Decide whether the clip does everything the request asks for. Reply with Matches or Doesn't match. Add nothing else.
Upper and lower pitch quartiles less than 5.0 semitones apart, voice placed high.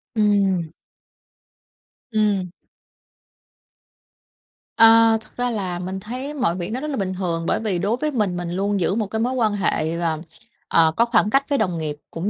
Matches